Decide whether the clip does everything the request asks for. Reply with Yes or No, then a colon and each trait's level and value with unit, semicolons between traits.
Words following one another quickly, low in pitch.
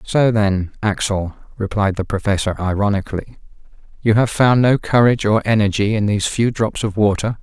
No: average, 160 wpm; low, 105 Hz